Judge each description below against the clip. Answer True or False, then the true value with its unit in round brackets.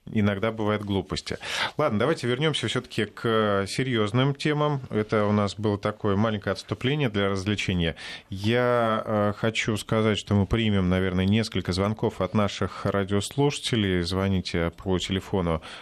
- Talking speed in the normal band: True (135 wpm)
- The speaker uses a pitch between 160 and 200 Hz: False (105 Hz)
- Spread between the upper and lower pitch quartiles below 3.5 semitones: True (2.7 semitones)